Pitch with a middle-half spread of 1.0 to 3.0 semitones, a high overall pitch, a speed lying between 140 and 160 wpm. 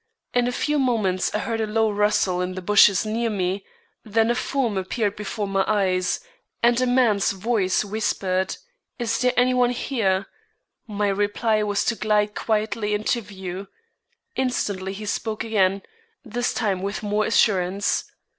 Yes: average, 2.7 semitones; high, 210 Hz; average, 155 wpm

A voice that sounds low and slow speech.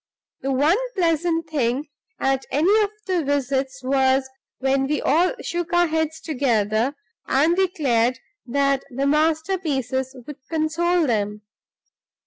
No: very high, 285 Hz; slow, 120 wpm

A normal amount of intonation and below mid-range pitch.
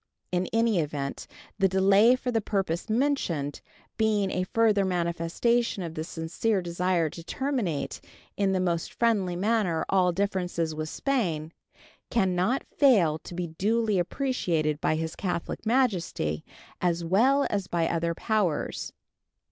No: average, 4.8 semitones; medium, 185 Hz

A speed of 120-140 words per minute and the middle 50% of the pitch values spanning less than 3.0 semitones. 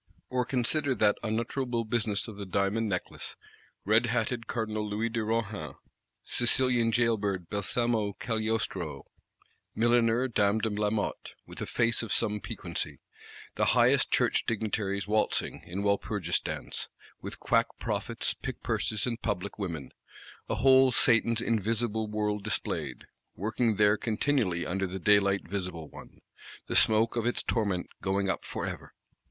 Yes: slow, 135 wpm; narrow, 2.5 semitones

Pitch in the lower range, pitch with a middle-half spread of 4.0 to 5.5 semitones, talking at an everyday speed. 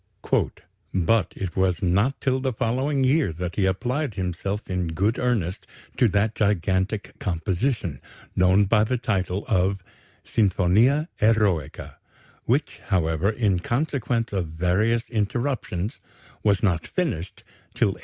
No: low, 100 Hz; average, 4.4 semitones; slow, 125 wpm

